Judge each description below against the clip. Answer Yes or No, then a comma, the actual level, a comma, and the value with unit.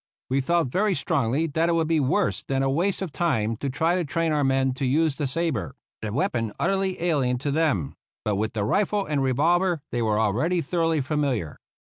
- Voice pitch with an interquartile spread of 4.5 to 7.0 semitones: Yes, average, 4.8 semitones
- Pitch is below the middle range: No, medium, 145 Hz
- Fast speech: Yes, fast, 215 wpm